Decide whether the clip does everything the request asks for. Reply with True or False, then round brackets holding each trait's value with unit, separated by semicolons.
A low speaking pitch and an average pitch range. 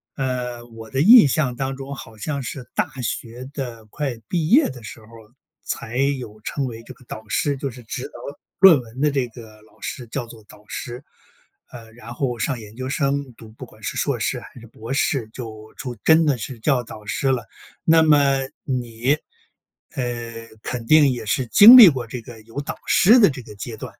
True (125 Hz; 3.5 semitones)